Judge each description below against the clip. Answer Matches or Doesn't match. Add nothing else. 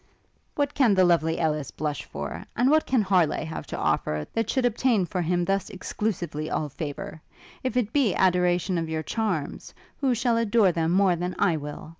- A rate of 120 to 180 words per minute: Doesn't match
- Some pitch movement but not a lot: Doesn't match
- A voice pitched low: Doesn't match